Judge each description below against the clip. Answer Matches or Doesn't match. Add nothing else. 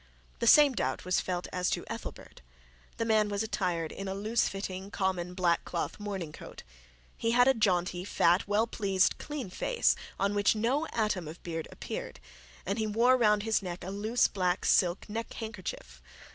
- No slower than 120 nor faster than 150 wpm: Doesn't match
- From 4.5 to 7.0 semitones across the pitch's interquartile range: Doesn't match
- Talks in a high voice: Matches